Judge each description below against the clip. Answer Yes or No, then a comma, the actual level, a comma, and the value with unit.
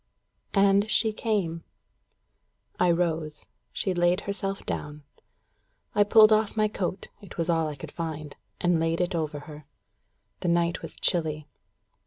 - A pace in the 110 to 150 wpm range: Yes, average, 145 wpm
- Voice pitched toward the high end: No, medium, 175 Hz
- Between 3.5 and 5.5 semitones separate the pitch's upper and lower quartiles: Yes, average, 3.8 semitones